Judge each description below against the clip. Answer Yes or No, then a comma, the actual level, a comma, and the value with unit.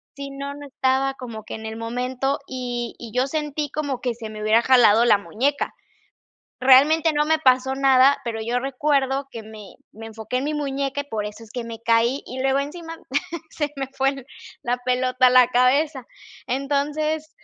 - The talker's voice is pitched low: No, very high, 260 Hz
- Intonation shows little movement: No, average, 3.0 semitones